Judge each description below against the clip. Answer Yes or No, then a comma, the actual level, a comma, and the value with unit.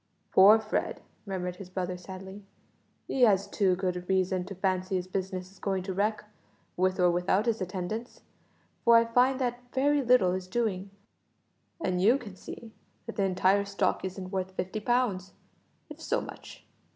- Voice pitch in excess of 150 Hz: Yes, high, 190 Hz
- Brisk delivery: No, average, 165 wpm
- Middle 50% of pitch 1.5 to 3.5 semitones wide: Yes, average, 3.0 semitones